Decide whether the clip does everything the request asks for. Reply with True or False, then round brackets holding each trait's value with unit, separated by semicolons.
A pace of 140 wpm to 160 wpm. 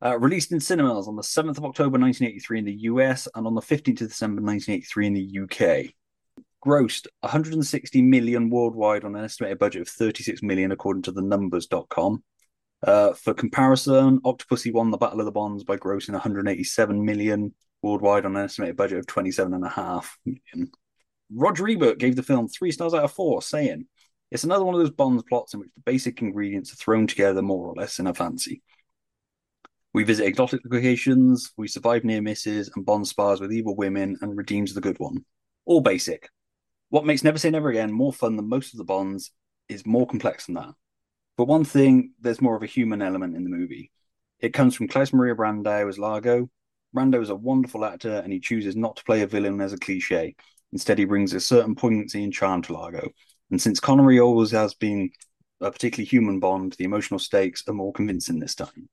False (200 wpm)